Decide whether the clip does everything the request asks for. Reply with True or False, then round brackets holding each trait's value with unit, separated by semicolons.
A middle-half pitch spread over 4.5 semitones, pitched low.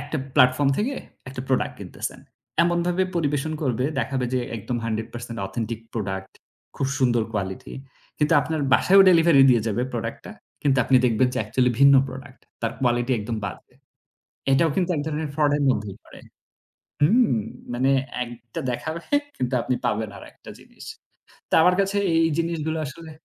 True (5.0 semitones; 130 Hz)